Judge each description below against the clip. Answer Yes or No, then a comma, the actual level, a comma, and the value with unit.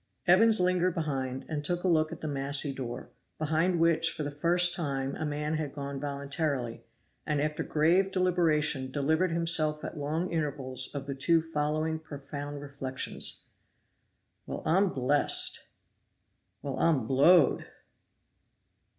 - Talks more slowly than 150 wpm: Yes, slow, 135 wpm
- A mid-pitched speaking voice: Yes, medium, 150 Hz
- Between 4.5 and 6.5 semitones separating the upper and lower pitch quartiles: No, average, 2.9 semitones